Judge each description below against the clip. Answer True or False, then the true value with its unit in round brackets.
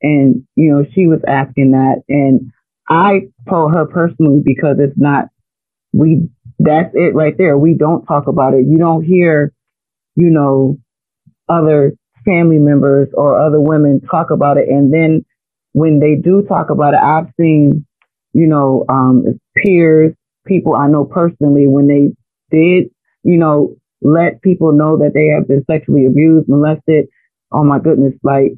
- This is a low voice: False (150 Hz)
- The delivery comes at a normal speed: True (160 wpm)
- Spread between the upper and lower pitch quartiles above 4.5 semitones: False (2.5 semitones)